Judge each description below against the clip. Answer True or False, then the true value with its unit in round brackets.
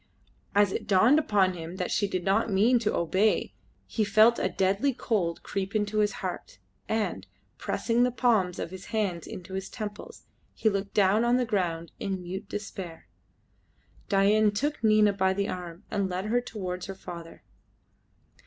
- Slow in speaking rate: False (170 wpm)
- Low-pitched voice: False (200 Hz)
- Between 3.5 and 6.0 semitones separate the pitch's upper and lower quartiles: False (2.7 semitones)